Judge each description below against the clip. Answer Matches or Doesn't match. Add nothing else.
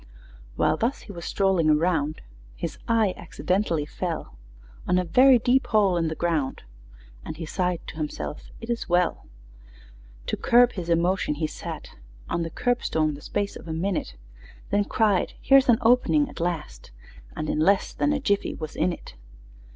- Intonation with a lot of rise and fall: Matches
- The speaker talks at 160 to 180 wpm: Matches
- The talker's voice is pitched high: Doesn't match